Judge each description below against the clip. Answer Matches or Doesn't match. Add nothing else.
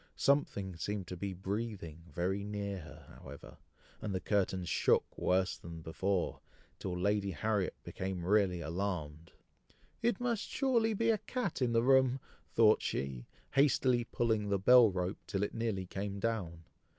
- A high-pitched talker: Doesn't match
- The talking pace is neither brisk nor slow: Matches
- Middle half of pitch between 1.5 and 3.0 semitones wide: Doesn't match